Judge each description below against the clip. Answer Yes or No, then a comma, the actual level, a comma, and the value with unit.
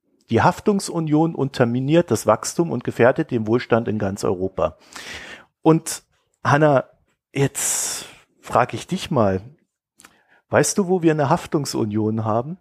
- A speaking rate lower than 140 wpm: Yes, slow, 125 wpm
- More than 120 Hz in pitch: Yes, low, 135 Hz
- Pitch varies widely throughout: Yes, wide, 6.5 semitones